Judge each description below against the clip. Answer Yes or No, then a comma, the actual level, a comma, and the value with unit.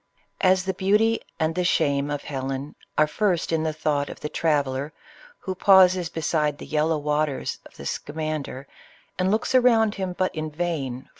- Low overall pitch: No, medium, 155 Hz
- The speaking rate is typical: Yes, average, 175 wpm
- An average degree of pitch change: Yes, average, 4.1 semitones